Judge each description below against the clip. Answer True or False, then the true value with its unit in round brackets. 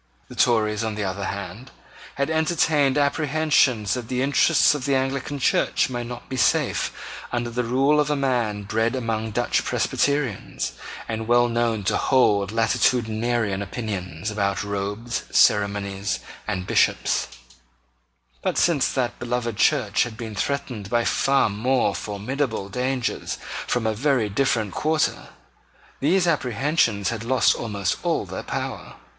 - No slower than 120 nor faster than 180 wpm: True (140 wpm)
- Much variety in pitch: False (4.3 semitones)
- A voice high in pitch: False (120 Hz)